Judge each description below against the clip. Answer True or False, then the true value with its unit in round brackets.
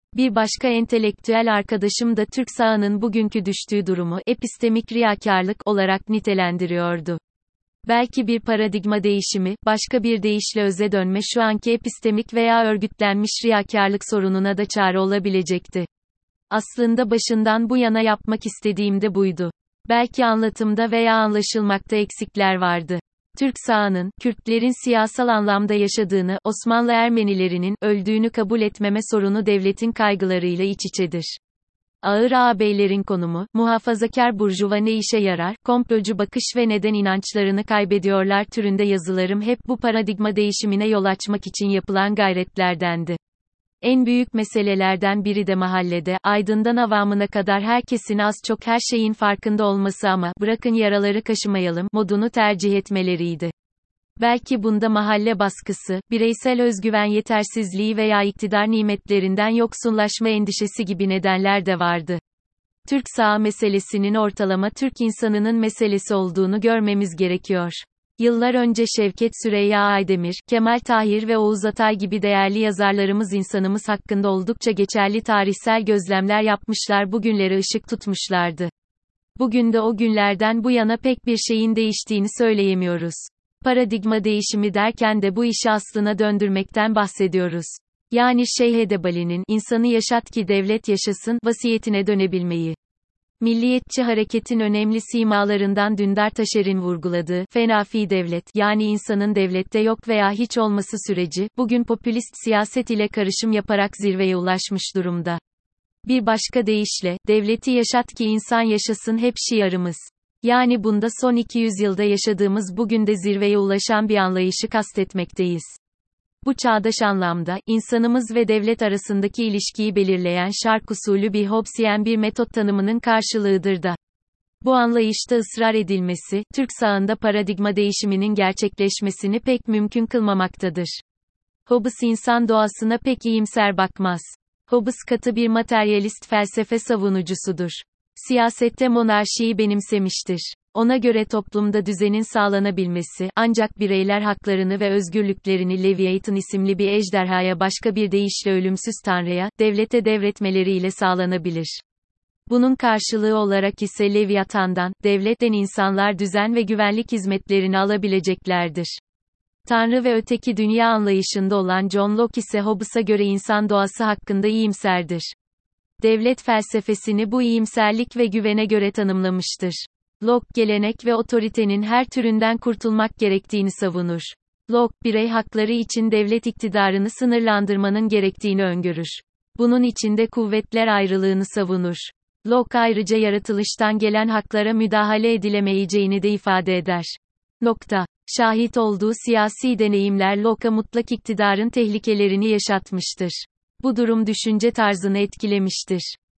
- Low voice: False (210 Hz)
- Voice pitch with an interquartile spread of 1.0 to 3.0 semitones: True (2.4 semitones)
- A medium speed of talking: True (120 wpm)